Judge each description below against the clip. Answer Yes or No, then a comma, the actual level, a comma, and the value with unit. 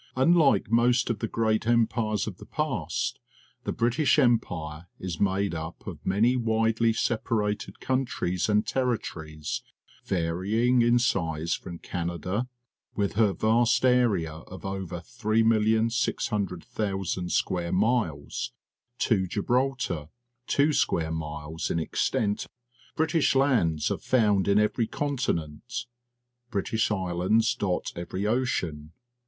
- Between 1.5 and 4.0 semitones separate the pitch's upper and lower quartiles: No, average, 5.2 semitones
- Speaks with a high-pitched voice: No, low, 105 Hz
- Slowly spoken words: Yes, slow, 115 wpm